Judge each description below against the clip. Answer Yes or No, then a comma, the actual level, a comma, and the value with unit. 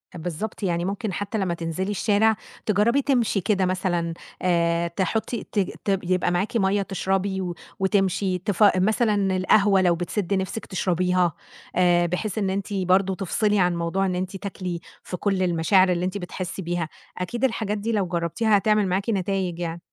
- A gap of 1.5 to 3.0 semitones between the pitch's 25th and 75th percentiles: Yes, narrow, 2.4 semitones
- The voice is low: No, high, 190 Hz